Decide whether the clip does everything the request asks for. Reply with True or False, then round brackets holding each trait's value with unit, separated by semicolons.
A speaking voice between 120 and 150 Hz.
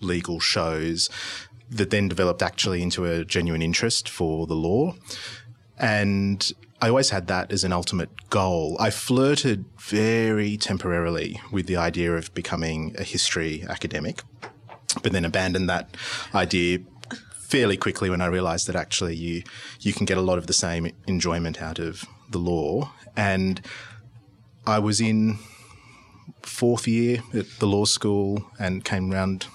False (95 Hz)